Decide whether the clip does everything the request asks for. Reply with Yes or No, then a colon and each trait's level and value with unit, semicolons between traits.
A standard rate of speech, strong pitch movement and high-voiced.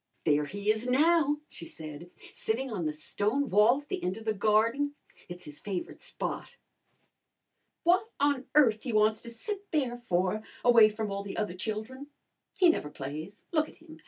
Yes: average, 180 wpm; wide, 6.4 semitones; high, 220 Hz